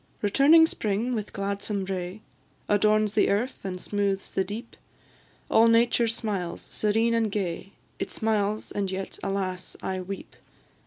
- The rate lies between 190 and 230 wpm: No, average, 140 wpm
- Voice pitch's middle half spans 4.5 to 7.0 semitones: No, narrow, 2.4 semitones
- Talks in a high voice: Yes, high, 205 Hz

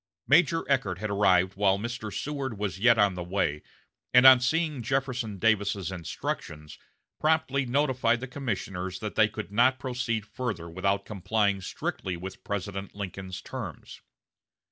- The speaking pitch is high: No, low, 105 Hz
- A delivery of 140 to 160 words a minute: Yes, average, 145 wpm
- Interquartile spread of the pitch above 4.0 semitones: Yes, average, 5.0 semitones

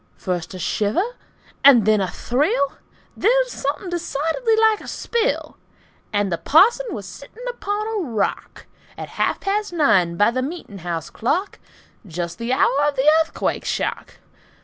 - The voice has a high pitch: Yes, very high, 280 Hz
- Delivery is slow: No, average, 150 wpm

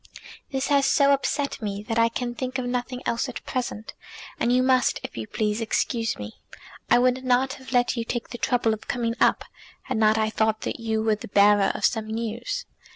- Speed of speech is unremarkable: No, fast, 215 wpm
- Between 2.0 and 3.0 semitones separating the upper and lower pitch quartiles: Yes, average, 2.7 semitones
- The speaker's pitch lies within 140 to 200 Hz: No, high, 240 Hz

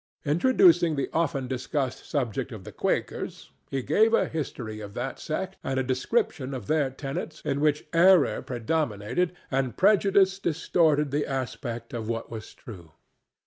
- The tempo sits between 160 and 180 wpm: No, average, 150 wpm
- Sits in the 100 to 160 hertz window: Yes, medium, 140 Hz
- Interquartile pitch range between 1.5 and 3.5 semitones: No, average, 5.1 semitones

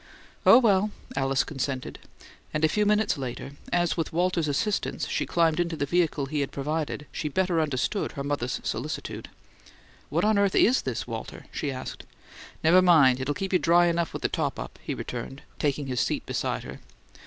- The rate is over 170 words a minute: Yes, average, 185 wpm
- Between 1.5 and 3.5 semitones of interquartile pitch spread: No, average, 4.5 semitones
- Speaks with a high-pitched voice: No, medium, 160 Hz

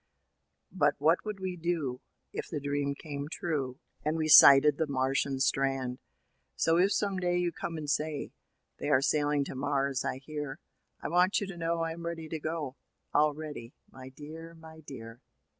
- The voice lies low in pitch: No, medium, 150 Hz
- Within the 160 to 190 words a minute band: Yes, average, 180 wpm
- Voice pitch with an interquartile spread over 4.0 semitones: No, average, 3.2 semitones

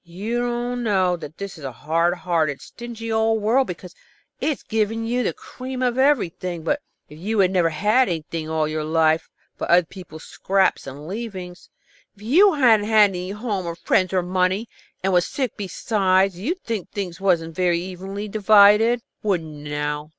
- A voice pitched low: No, high, 190 Hz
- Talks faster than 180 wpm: No, average, 175 wpm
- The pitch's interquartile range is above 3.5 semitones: Yes, average, 4.8 semitones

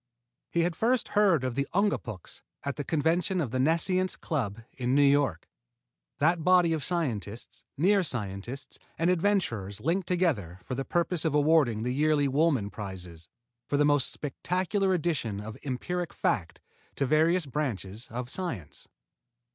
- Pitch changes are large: Yes, wide, 6.6 semitones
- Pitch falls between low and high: Yes, medium, 145 Hz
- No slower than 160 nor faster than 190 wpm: No, average, 150 wpm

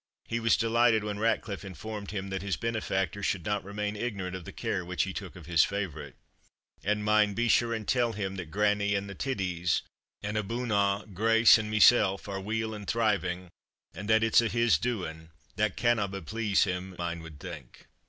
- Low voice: Yes, low, 100 Hz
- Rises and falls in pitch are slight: No, average, 3.0 semitones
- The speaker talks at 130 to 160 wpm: No, average, 195 wpm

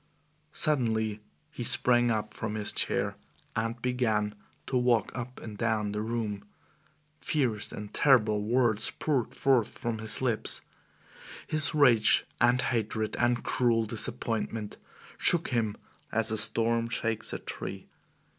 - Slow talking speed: Yes, slow, 130 wpm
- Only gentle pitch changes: Yes, narrow, 2.2 semitones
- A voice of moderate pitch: No, low, 115 Hz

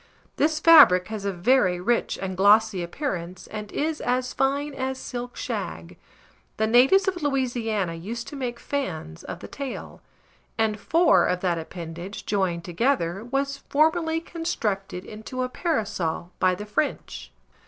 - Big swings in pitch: Yes, wide, 7.1 semitones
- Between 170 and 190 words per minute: No, average, 145 wpm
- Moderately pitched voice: No, high, 225 Hz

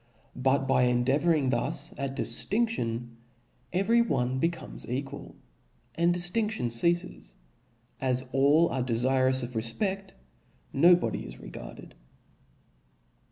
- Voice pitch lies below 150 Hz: Yes, low, 135 Hz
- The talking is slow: Yes, slow, 110 wpm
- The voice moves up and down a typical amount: No, wide, 5.9 semitones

